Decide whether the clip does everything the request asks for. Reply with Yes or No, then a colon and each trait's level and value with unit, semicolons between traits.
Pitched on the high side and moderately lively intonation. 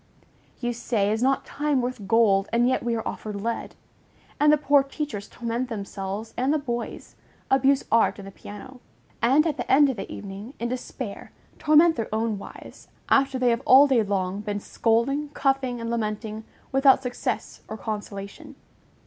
Yes: high, 235 Hz; average, 4.2 semitones